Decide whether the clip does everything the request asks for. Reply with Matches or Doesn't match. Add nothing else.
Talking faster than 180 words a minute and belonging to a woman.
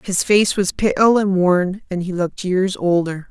Matches